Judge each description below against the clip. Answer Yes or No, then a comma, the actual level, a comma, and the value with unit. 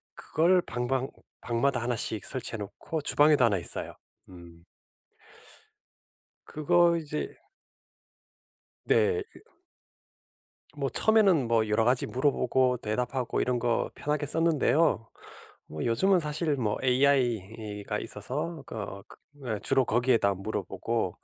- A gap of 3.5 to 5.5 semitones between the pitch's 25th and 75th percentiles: Yes, average, 5.1 semitones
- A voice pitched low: Yes, low, 125 Hz